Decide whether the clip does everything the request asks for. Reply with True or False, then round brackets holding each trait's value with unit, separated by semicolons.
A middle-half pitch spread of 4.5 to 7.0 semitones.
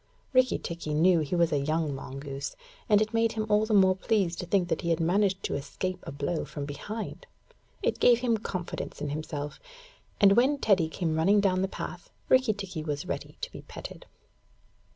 True (5.3 semitones)